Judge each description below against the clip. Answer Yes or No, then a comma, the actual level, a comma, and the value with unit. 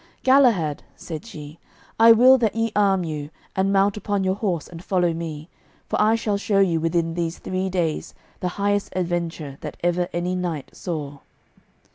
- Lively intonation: No, average, 3.6 semitones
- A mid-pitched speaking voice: Yes, medium, 180 Hz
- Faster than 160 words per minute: Yes, average, 170 wpm